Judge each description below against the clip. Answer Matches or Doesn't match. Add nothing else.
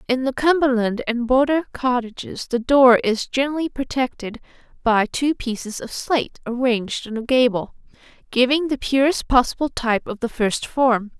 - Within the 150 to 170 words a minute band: Matches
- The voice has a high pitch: Matches